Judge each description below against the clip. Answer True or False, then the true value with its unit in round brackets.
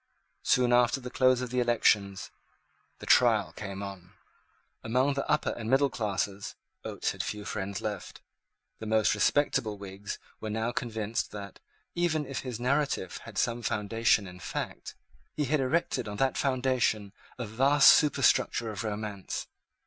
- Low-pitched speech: True (115 Hz)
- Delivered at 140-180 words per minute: True (150 wpm)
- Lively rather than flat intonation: False (4.0 semitones)